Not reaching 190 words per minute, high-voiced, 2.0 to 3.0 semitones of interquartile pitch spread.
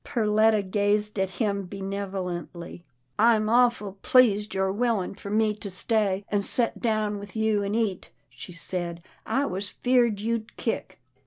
Yes: average, 165 wpm; high, 205 Hz; narrow, 2.4 semitones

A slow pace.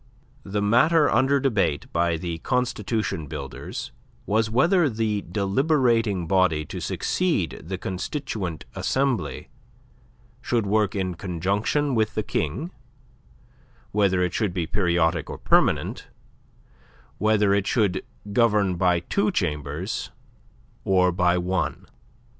Yes: slow, 115 wpm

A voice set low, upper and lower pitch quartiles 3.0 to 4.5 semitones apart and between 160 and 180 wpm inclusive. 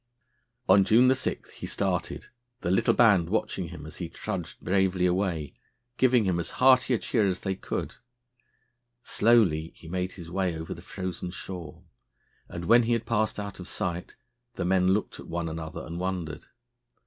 Yes: very low, 95 Hz; average, 3.6 semitones; average, 170 wpm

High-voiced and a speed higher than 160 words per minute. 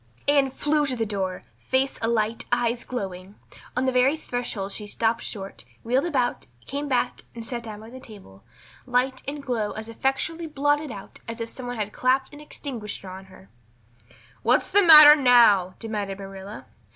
Yes: high, 240 Hz; average, 175 wpm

